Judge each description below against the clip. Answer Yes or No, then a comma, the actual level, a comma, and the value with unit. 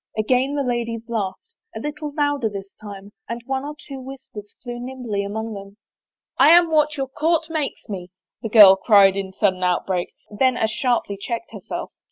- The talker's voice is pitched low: No, high, 235 Hz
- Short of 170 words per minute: No, average, 185 wpm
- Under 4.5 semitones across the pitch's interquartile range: No, wide, 5.5 semitones